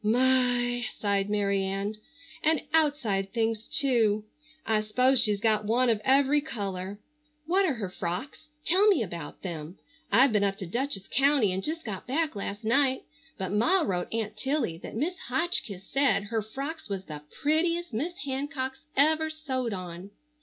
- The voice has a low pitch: No, high, 235 Hz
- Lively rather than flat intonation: Yes, wide, 5.9 semitones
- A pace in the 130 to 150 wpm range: No, average, 160 wpm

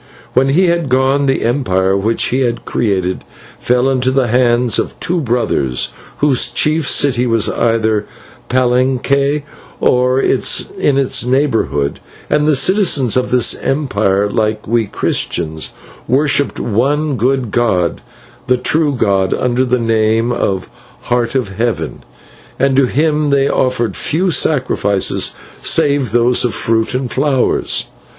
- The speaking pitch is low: Yes, low, 125 Hz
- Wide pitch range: No, average, 3.4 semitones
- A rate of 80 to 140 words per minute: Yes, slow, 135 wpm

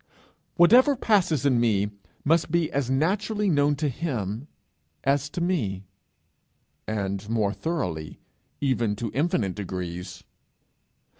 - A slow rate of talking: Yes, slow, 115 wpm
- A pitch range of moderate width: No, wide, 8.4 semitones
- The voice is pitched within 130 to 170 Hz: Yes, low, 135 Hz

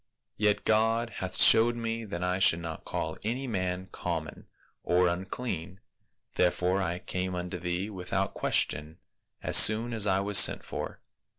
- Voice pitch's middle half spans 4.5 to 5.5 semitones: No, average, 3.4 semitones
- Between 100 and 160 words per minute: Yes, average, 155 wpm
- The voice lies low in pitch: Yes, very low, 95 Hz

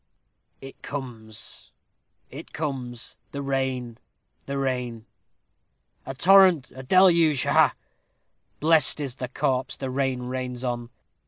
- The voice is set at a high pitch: No, low, 130 Hz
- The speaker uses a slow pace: Yes, slow, 115 wpm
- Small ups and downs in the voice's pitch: Yes, narrow, 2.1 semitones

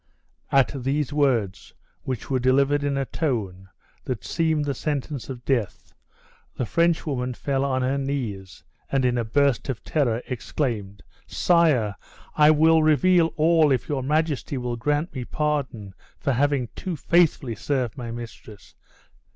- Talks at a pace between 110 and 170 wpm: Yes, average, 150 wpm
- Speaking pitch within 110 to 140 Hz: Yes, low, 135 Hz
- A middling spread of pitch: Yes, average, 3.8 semitones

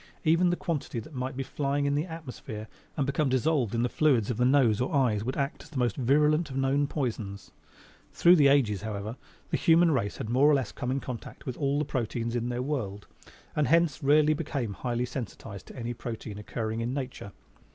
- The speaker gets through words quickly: Yes, fast, 215 wpm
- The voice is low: Yes, low, 130 Hz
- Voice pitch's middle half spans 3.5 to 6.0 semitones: Yes, average, 4.0 semitones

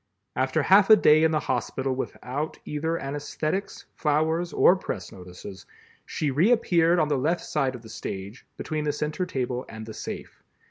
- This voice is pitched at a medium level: Yes, medium, 150 Hz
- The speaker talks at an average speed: Yes, average, 170 wpm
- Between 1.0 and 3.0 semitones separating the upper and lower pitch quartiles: No, average, 4.0 semitones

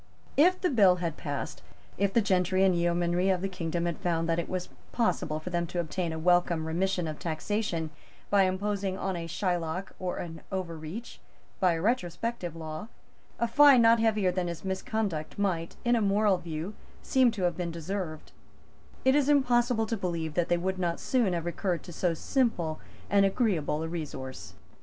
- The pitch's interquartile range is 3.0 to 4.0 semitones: Yes, average, 3.7 semitones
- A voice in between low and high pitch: Yes, medium, 180 Hz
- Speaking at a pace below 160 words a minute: No, average, 180 wpm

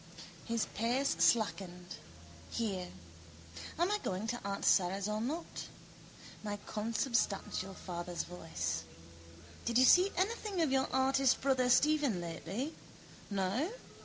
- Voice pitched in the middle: No, high, 230 Hz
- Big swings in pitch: Yes, wide, 6.3 semitones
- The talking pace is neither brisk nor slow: No, slow, 115 wpm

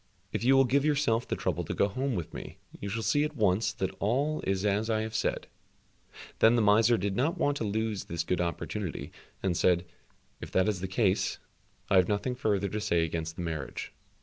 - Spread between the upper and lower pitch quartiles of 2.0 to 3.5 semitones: No, average, 4.3 semitones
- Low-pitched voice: Yes, low, 105 Hz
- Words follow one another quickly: Yes, fast, 215 wpm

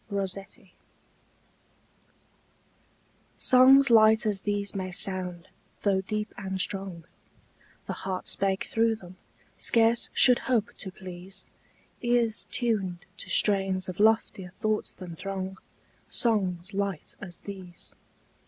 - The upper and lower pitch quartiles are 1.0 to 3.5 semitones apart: Yes, average, 2.8 semitones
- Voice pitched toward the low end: No, high, 195 Hz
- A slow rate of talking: Yes, slow, 110 wpm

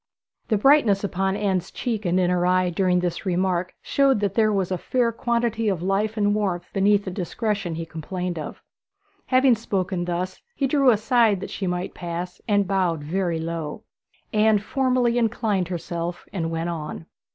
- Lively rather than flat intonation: No, average, 3.6 semitones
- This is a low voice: No, high, 190 Hz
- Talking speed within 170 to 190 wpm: Yes, average, 175 wpm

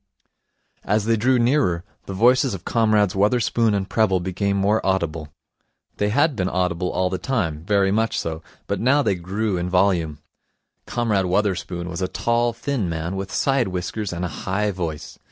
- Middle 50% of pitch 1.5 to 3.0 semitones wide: No, average, 3.8 semitones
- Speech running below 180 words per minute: Yes, average, 170 wpm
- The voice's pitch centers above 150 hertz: No, low, 100 Hz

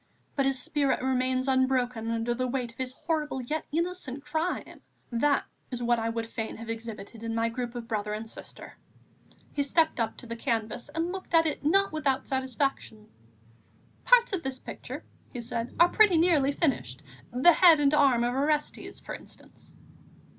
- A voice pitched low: No, very high, 260 Hz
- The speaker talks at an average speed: Yes, average, 175 wpm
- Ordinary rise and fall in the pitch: Yes, average, 4.5 semitones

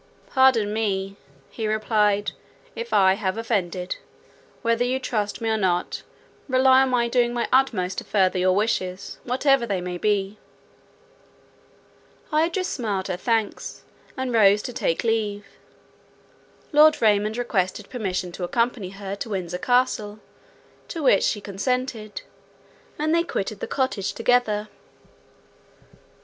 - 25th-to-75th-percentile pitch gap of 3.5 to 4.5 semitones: Yes, average, 4.1 semitones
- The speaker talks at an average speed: No, slow, 130 wpm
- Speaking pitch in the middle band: No, high, 215 Hz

